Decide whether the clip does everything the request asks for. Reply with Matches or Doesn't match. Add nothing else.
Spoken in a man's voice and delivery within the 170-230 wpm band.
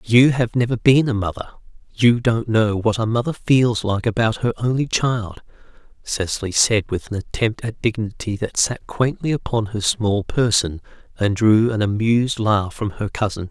Matches